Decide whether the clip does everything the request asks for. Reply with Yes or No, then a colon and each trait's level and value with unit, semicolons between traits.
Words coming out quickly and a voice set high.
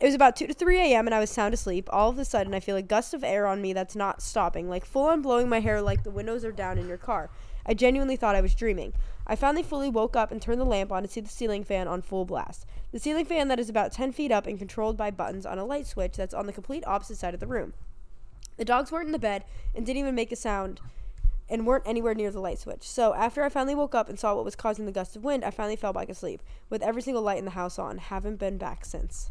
Yes: fast, 290 wpm; high, 220 Hz